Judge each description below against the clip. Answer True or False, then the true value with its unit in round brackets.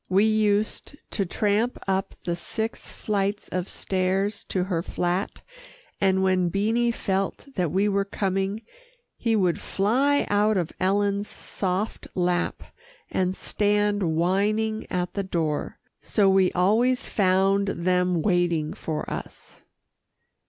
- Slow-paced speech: True (125 wpm)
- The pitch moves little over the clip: True (2.3 semitones)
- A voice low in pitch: False (195 Hz)